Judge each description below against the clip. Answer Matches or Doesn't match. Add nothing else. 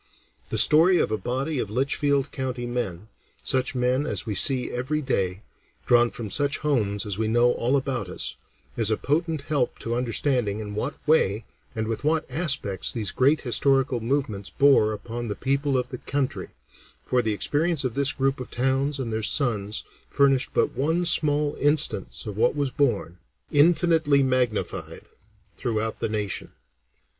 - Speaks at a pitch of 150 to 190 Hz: Doesn't match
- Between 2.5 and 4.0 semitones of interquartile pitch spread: Doesn't match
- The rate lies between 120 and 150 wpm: Doesn't match